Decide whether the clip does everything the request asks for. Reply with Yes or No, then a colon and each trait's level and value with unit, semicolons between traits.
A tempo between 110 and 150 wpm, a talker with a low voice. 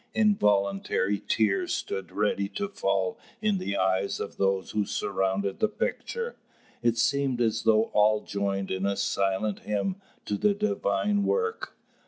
Yes: average, 145 wpm; low, 105 Hz